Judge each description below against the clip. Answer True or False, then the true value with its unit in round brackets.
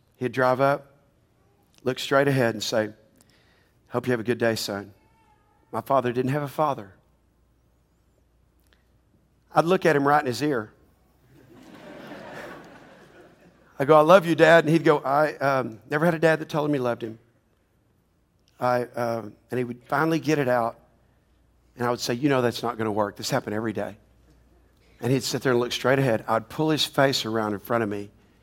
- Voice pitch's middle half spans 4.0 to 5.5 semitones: True (4.5 semitones)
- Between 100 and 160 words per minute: False (190 wpm)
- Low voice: True (120 Hz)